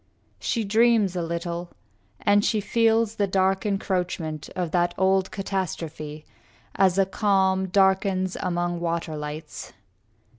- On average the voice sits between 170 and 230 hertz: Yes, high, 190 Hz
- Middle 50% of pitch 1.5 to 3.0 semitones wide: Yes, narrow, 2.4 semitones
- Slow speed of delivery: Yes, slow, 120 wpm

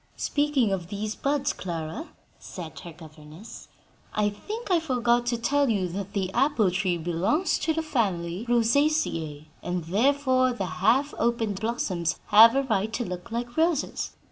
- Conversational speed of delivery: Yes, average, 155 wpm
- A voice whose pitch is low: No, high, 225 Hz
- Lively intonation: Yes, wide, 6.9 semitones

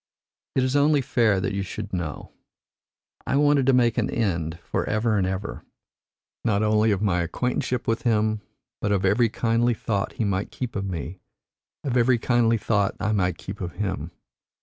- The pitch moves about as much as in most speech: Yes, average, 3.8 semitones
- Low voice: Yes, low, 105 Hz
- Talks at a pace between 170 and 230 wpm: Yes, average, 180 wpm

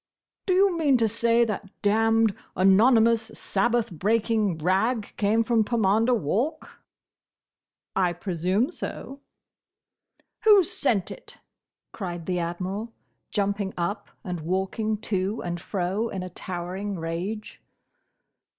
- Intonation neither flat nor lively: Yes, average, 3.8 semitones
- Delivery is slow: Yes, slow, 115 wpm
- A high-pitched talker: Yes, high, 205 Hz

